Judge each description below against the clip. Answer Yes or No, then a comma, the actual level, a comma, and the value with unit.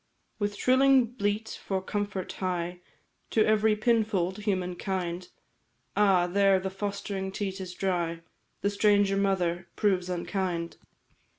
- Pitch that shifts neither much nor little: No, narrow, 2.3 semitones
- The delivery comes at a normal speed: No, slow, 115 wpm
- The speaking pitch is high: Yes, high, 195 Hz